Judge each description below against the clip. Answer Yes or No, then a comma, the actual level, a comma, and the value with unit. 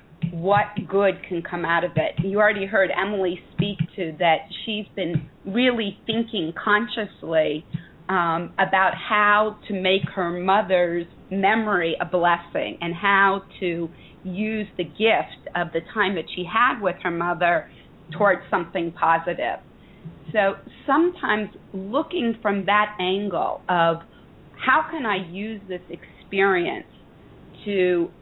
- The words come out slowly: Yes, slow, 130 wpm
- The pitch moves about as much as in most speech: Yes, average, 3.2 semitones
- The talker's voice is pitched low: No, high, 190 Hz